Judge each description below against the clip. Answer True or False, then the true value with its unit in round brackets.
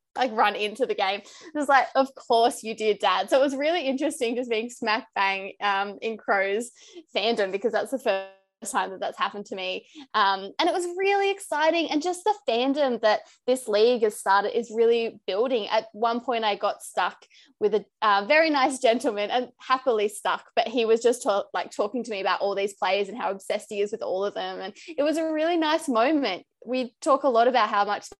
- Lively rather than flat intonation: True (6.1 semitones)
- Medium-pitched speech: False (235 Hz)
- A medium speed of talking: False (225 wpm)